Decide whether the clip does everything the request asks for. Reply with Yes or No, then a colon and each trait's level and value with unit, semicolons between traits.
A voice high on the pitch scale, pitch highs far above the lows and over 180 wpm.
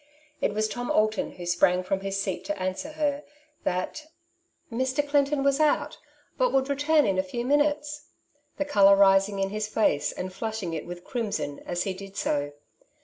Yes: high, 215 Hz; wide, 7.2 semitones; average, 190 wpm